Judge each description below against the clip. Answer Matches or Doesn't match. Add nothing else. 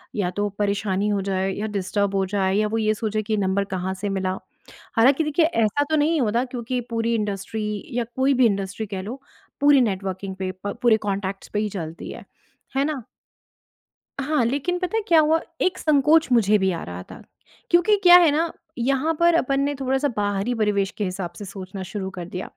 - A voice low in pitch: Doesn't match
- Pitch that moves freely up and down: Matches